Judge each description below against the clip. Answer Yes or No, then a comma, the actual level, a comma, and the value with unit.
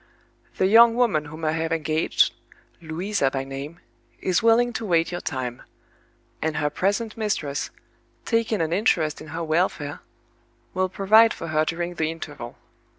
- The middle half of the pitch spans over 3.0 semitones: Yes, average, 4.7 semitones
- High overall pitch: No, medium, 165 Hz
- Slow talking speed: No, average, 150 wpm